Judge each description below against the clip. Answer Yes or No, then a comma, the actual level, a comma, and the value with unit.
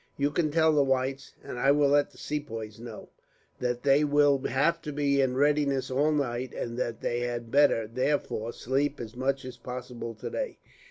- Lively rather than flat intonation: No, average, 3.1 semitones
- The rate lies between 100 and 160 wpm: No, average, 185 wpm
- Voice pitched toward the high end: No, low, 135 Hz